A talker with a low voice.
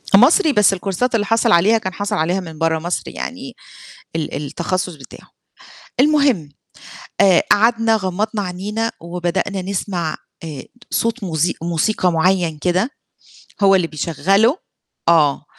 No: medium, 185 Hz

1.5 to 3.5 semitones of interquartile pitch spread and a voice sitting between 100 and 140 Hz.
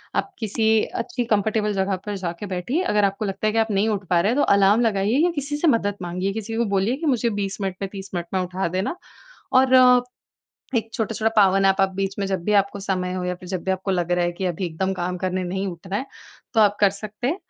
No: average, 2.8 semitones; high, 195 Hz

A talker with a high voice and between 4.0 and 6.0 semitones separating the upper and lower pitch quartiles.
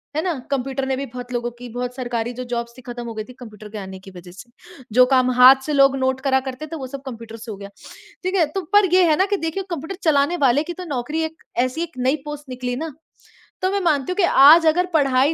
Yes: very high, 265 Hz; average, 4.5 semitones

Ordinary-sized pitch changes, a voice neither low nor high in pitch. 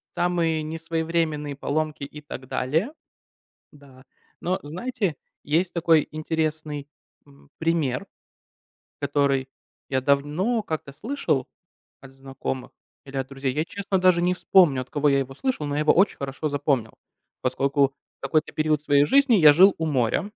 Yes: average, 3.3 semitones; medium, 150 Hz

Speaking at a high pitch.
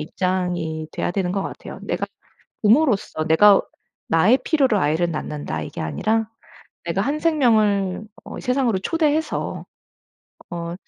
Yes: high, 195 Hz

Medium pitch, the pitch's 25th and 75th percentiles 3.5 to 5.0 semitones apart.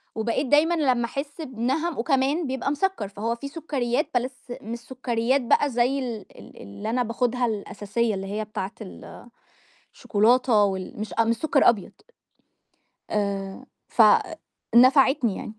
No: high, 240 Hz; average, 3.8 semitones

